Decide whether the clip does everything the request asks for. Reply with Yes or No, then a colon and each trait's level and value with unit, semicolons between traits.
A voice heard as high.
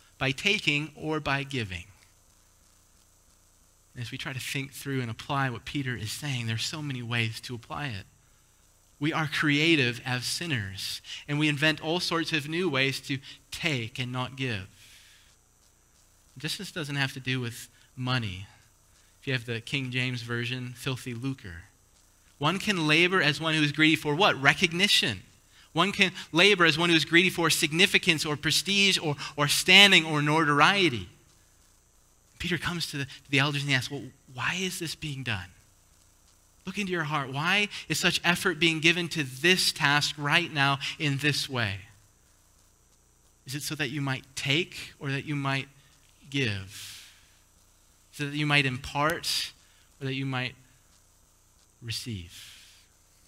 No: low, 135 Hz